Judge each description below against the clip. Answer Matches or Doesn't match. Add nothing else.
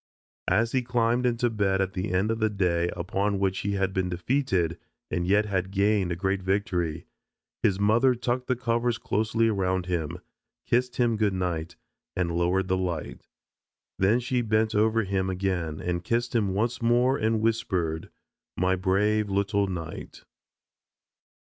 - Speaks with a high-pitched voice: Doesn't match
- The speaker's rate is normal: Matches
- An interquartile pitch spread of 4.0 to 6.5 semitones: Doesn't match